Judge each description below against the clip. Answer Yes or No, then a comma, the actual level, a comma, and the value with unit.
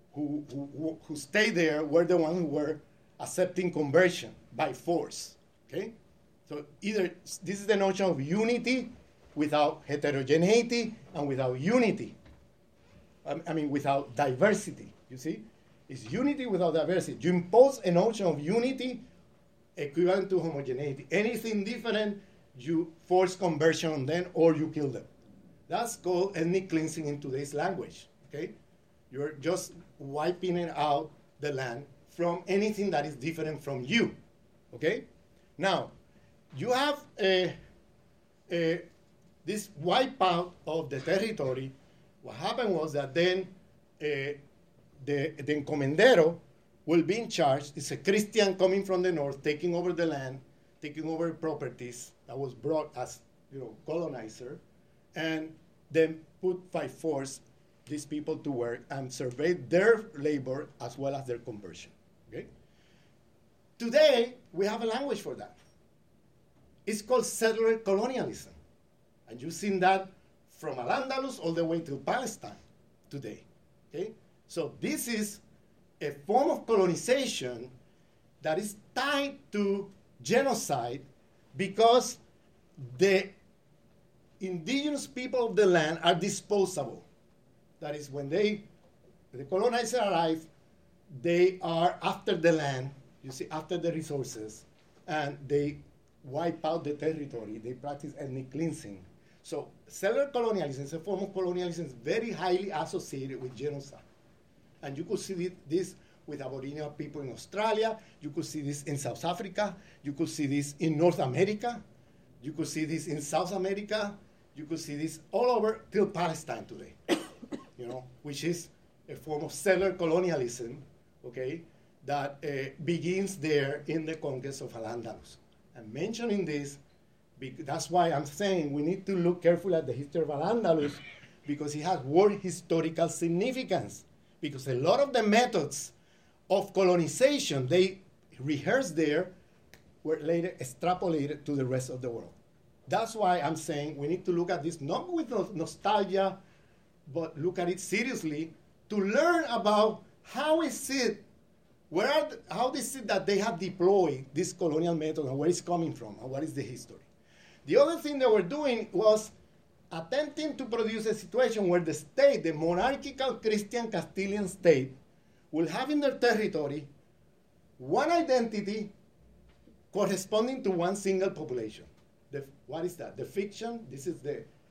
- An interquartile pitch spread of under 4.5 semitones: No, average, 5.1 semitones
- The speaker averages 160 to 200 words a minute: No, average, 145 wpm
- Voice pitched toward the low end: No, medium, 170 Hz